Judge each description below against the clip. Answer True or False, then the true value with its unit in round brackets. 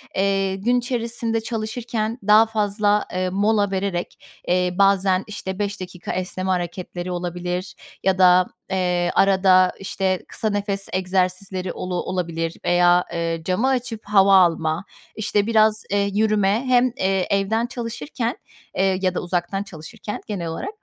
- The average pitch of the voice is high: True (195 Hz)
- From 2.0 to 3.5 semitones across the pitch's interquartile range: True (2.8 semitones)